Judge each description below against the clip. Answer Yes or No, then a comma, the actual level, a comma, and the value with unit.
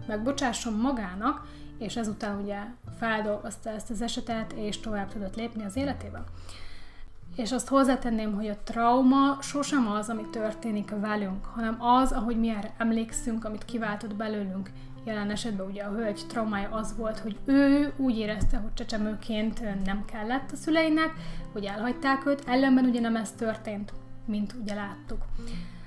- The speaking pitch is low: No, high, 220 Hz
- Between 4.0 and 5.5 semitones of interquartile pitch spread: No, average, 2.8 semitones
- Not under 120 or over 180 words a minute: Yes, average, 150 wpm